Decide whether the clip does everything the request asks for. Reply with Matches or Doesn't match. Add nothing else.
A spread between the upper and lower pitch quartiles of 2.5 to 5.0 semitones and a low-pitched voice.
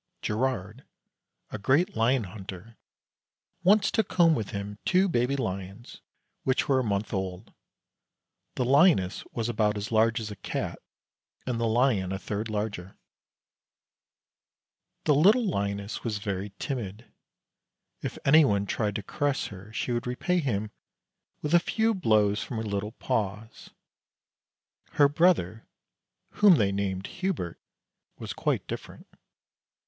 Doesn't match